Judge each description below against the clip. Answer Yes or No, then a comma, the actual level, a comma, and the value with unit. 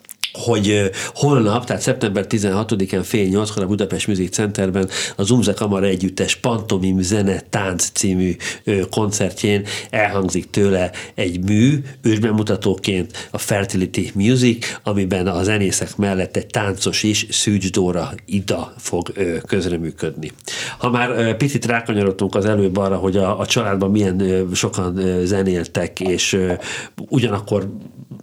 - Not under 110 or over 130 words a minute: Yes, average, 120 wpm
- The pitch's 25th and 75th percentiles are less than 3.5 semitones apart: Yes, narrow, 2.6 semitones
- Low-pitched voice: Yes, low, 100 Hz